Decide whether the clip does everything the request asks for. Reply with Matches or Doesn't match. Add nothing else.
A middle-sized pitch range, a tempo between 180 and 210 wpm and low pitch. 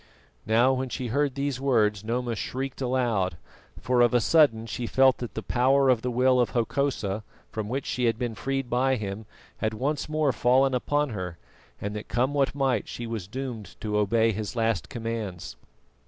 Matches